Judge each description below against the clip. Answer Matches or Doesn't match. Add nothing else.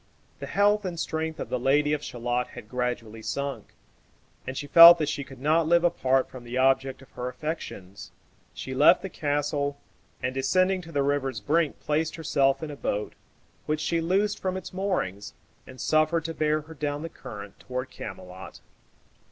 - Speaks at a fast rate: Doesn't match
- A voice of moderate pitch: Matches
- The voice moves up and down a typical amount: Matches